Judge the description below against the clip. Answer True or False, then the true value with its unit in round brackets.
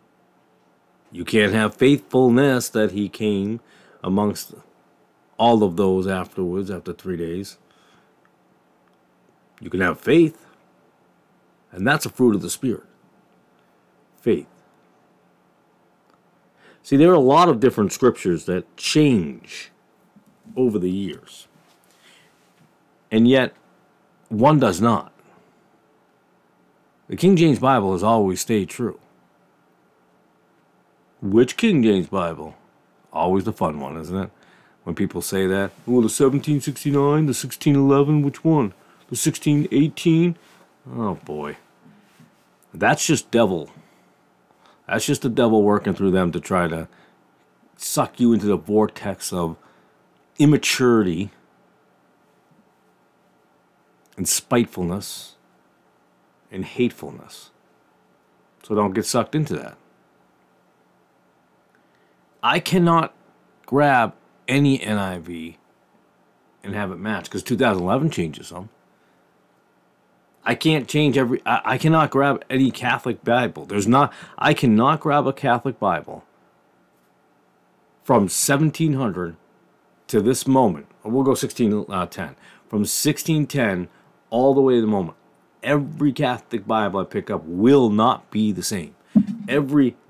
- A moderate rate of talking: False (115 wpm)